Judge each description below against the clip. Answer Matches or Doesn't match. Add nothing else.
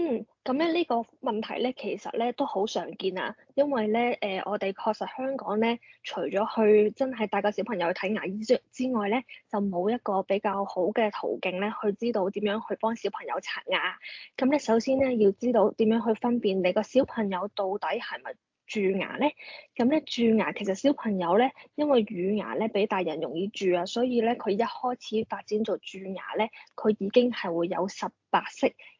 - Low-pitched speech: Doesn't match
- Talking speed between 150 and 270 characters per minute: Doesn't match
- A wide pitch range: Doesn't match